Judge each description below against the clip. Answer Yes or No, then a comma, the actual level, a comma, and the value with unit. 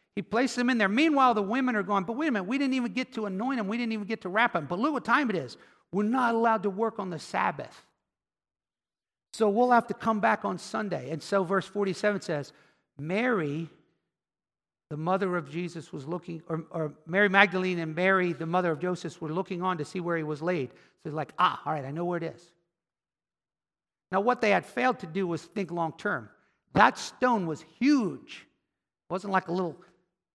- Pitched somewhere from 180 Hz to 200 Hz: Yes, high, 190 Hz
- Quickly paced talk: Yes, fast, 220 wpm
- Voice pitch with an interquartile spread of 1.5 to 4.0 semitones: No, average, 4.7 semitones